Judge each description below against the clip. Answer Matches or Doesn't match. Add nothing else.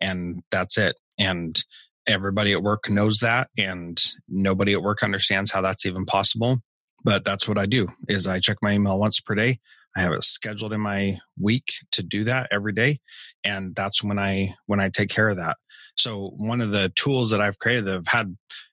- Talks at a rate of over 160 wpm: Matches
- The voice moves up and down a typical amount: Doesn't match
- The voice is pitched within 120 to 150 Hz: Doesn't match